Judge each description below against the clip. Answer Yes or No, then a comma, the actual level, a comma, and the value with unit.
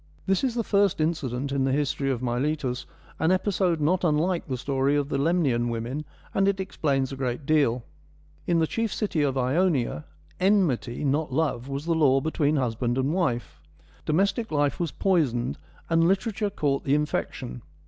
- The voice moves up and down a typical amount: Yes, average, 4.8 semitones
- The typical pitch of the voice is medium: Yes, medium, 145 Hz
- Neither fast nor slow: Yes, average, 170 wpm